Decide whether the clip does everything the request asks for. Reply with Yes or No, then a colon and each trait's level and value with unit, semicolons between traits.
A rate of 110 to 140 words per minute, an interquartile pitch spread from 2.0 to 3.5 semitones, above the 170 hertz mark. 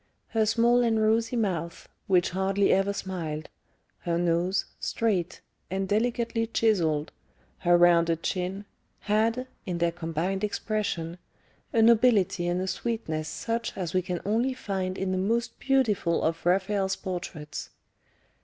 No: slow, 135 wpm; average, 4.2 semitones; high, 190 Hz